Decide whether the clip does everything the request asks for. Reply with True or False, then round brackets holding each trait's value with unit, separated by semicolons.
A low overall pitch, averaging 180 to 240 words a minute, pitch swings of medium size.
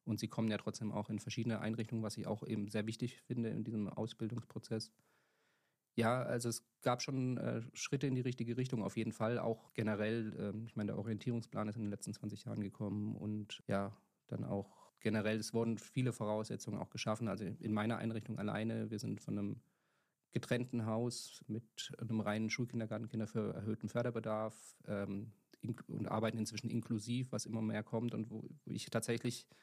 False (110 Hz; 185 wpm; 1.6 semitones)